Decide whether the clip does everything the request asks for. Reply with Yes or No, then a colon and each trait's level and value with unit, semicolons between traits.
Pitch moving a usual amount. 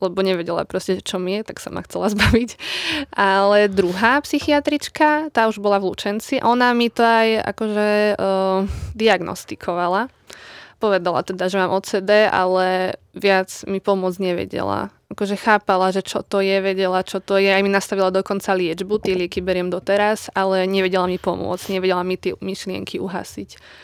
No: narrow, 2.1 semitones